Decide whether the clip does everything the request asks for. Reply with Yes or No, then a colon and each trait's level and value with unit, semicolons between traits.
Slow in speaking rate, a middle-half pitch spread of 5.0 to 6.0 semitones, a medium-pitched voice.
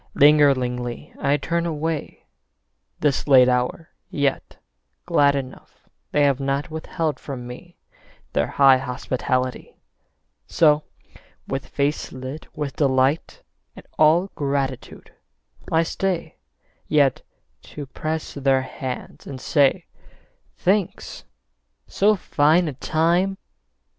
No: slow, 105 wpm; average, 3.2 semitones; medium, 145 Hz